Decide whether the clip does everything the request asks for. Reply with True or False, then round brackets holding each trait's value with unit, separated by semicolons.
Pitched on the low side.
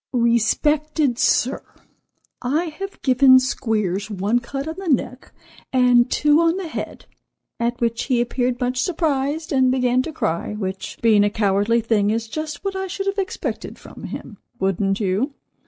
False (250 Hz)